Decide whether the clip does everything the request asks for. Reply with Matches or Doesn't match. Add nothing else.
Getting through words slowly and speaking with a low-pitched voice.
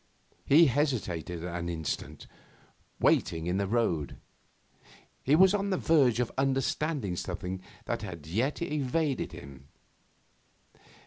Matches